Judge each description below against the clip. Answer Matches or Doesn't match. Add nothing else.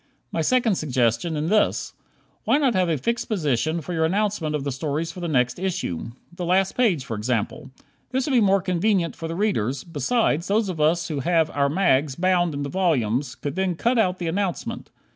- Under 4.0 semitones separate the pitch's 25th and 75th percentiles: Doesn't match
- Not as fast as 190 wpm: Doesn't match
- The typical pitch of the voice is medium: Matches